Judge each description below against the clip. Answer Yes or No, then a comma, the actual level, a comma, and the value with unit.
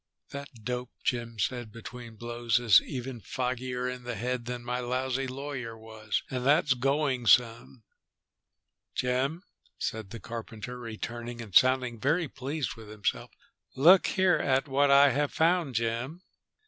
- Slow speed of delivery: No, average, 145 wpm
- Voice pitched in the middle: No, low, 125 Hz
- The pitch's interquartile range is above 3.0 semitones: No, narrow, 2.5 semitones